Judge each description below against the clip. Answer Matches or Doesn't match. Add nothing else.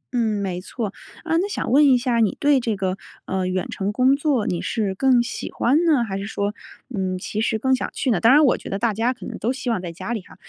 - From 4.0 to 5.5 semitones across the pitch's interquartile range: Matches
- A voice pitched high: Matches